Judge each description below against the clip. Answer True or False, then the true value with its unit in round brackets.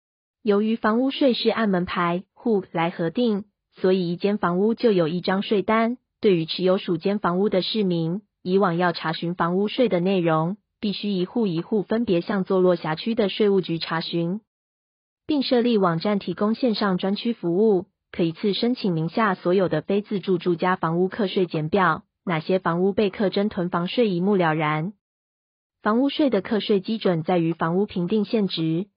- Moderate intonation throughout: True (3.5 semitones)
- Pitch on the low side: False (195 Hz)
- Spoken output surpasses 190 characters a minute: True (270 characters per minute)